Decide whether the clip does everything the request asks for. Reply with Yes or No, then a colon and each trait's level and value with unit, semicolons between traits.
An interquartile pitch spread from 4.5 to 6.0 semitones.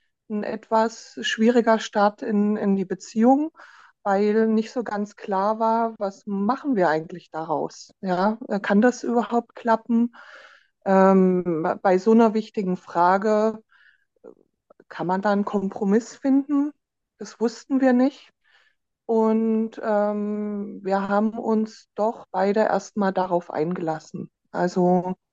No: average, 3.0 semitones